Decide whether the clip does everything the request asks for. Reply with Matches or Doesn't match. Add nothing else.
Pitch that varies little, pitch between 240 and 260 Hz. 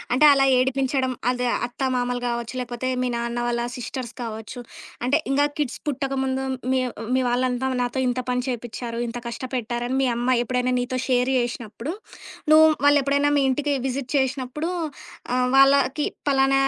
Matches